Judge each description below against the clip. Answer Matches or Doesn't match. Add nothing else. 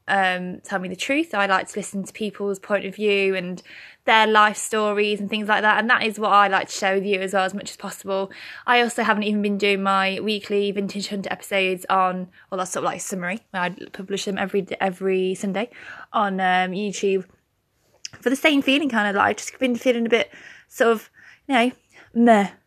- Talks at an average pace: Doesn't match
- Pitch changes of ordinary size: Doesn't match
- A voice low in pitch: Doesn't match